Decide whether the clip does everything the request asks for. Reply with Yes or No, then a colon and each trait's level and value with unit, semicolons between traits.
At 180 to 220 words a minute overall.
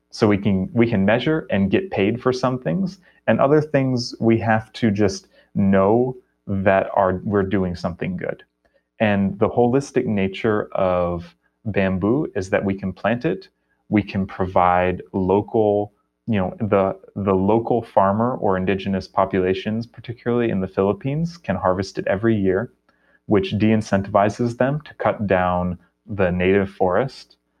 No: average, 150 wpm